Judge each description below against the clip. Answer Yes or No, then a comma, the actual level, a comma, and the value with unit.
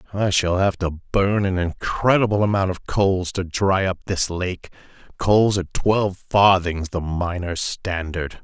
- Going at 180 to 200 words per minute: No, average, 150 wpm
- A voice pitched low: Yes, very low, 95 Hz